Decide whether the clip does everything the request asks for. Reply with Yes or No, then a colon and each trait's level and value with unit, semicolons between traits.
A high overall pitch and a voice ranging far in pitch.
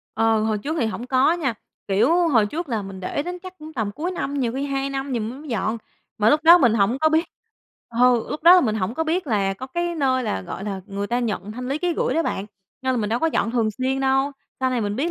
Yes: very high, 255 Hz; wide, 6.0 semitones